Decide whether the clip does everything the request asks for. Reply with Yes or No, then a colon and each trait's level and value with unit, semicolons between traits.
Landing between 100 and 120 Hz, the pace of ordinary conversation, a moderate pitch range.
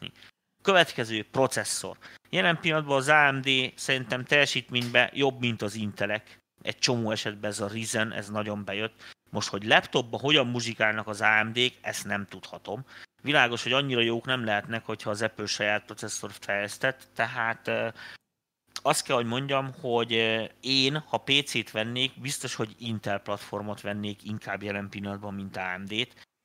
Yes: low, 115 Hz; average, 145 wpm; average, 3.6 semitones